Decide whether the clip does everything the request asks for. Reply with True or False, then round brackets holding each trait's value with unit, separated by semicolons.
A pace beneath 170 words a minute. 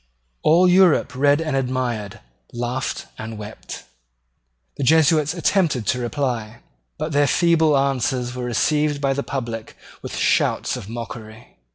True (135 wpm)